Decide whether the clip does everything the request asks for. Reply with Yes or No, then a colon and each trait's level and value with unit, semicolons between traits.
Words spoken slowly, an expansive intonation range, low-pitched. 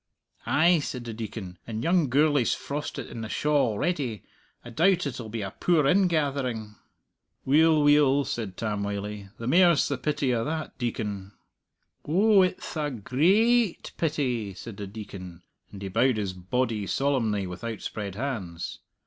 No: average, 155 wpm; wide, 6.3 semitones; low, 125 Hz